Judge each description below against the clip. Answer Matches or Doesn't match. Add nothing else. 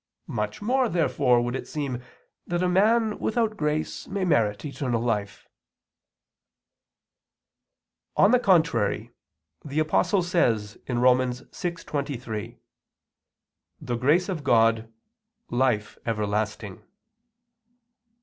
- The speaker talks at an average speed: Doesn't match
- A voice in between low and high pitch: Doesn't match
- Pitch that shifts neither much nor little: Doesn't match